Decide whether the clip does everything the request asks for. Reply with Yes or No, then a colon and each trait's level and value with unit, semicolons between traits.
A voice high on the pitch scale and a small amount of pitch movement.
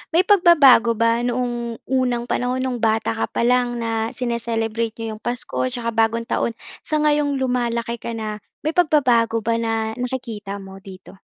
Yes: high, 235 Hz; narrow, 1.9 semitones